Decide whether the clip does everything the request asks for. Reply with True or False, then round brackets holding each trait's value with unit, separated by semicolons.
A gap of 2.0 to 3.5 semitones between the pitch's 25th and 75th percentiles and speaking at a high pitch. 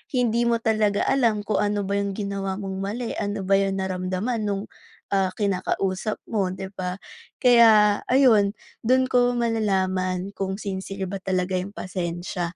True (2.4 semitones; 200 Hz)